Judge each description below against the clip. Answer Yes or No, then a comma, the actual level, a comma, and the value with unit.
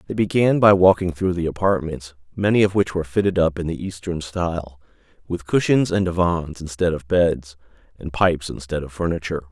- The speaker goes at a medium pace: Yes, average, 185 wpm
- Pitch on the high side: No, very low, 85 Hz